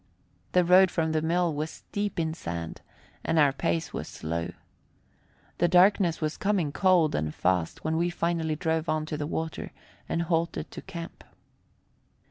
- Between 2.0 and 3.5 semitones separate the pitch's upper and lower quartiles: Yes, narrow, 2.4 semitones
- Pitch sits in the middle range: Yes, medium, 160 Hz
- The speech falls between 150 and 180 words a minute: Yes, average, 160 wpm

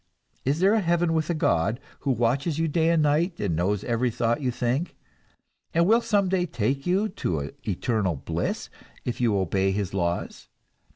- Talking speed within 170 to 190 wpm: Yes, average, 180 wpm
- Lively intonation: Yes, wide, 8.5 semitones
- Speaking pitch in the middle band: No, low, 130 Hz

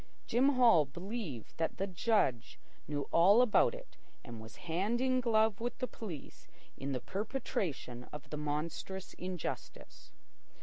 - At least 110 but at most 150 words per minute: Yes, average, 140 wpm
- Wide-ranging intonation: Yes, wide, 7.9 semitones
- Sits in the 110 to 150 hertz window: No, high, 190 Hz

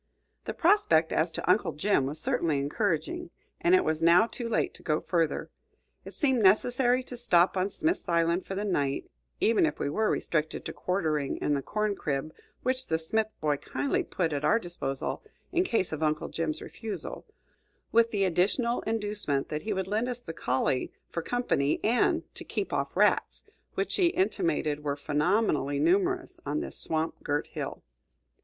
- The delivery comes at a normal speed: Yes, average, 175 wpm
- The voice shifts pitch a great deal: Yes, wide, 7.5 semitones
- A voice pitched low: No, medium, 185 Hz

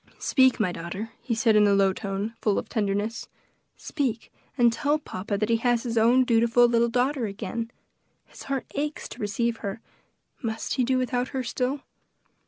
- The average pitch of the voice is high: Yes, high, 230 Hz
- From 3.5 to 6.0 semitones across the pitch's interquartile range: No, average, 2.9 semitones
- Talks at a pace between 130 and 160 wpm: No, average, 180 wpm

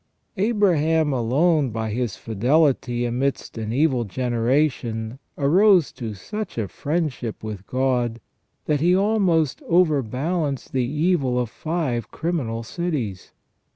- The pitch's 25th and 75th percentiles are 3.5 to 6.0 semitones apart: Yes, wide, 5.6 semitones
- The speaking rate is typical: No, slow, 115 wpm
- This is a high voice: No, low, 135 Hz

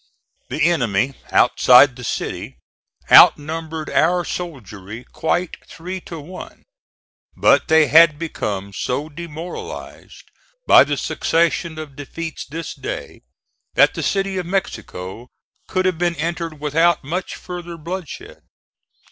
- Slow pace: Yes, slow, 120 wpm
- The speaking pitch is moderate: Yes, medium, 160 Hz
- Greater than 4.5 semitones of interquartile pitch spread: No, average, 3.7 semitones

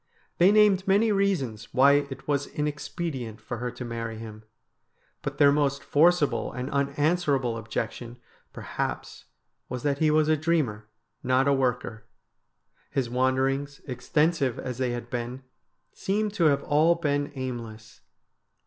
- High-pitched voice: No, low, 135 Hz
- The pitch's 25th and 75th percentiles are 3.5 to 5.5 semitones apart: Yes, average, 3.8 semitones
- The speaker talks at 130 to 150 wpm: Yes, average, 145 wpm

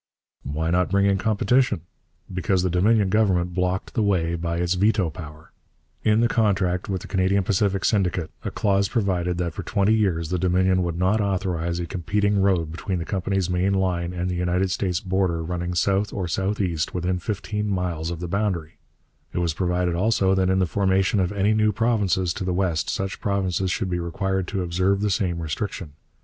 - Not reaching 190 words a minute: No, average, 195 wpm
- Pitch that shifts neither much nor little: No, narrow, 2.1 semitones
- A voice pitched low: Yes, very low, 95 Hz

